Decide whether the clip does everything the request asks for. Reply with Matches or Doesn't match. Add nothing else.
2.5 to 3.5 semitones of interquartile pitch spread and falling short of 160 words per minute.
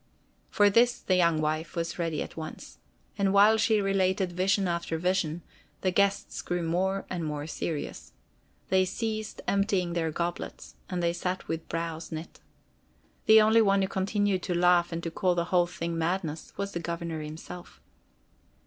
Doesn't match